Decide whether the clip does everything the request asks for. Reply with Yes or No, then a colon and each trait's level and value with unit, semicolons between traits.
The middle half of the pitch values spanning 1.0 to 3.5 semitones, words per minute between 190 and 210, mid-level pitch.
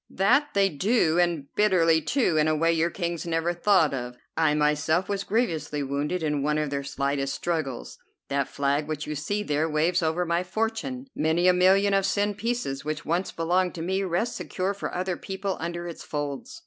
No: average, 4.2 semitones; average, 195 wpm; medium, 170 Hz